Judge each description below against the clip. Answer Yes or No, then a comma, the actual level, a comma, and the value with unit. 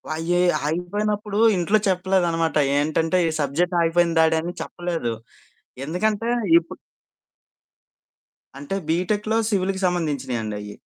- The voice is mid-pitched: Yes, medium, 175 Hz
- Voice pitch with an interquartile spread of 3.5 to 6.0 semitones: No, average, 3.1 semitones